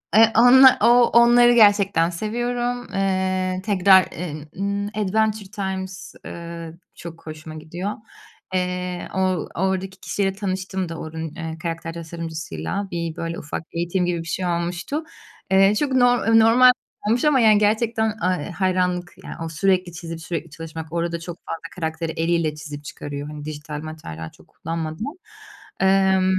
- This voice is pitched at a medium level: Yes, medium, 180 Hz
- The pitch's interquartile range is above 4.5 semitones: No, average, 3.8 semitones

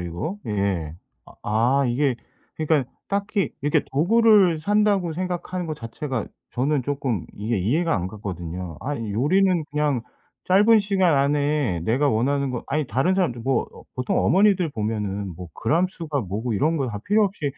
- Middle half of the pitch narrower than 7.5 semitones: No, wide, 7.9 semitones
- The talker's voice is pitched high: No, medium, 140 Hz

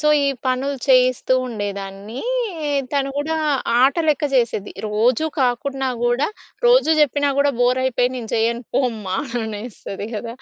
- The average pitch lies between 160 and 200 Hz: No, very high, 250 Hz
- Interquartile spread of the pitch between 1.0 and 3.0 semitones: No, average, 3.8 semitones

